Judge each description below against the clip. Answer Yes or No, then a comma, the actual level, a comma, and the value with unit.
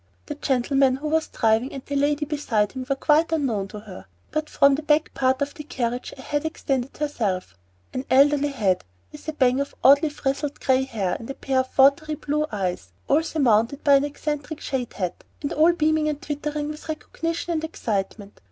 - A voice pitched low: No, very high, 280 Hz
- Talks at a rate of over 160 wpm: Yes, average, 200 wpm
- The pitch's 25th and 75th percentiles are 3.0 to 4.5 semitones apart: Yes, average, 3.3 semitones